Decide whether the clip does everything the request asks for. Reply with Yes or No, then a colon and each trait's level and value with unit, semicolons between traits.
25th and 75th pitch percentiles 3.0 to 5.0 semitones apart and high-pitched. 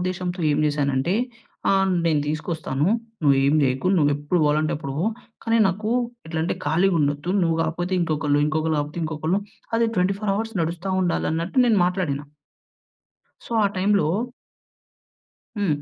No: average, 3.8 semitones; medium, 165 Hz